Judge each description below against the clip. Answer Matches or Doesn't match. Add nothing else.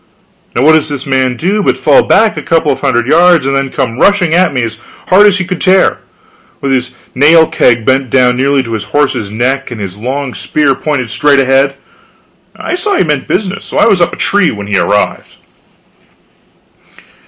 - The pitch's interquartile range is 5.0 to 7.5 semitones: Matches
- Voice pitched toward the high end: Doesn't match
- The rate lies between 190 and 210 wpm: Matches